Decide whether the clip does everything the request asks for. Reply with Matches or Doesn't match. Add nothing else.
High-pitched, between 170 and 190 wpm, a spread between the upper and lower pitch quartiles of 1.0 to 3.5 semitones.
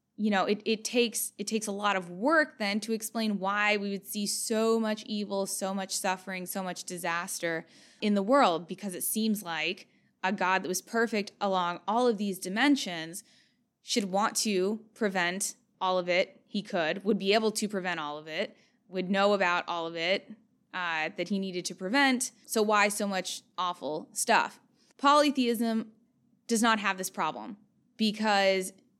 Matches